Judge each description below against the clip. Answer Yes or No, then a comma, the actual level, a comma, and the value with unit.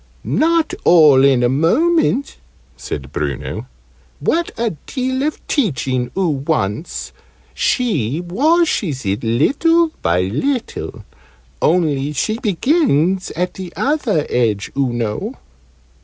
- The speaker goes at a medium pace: No, slow, 110 wpm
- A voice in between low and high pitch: Yes, medium, 170 Hz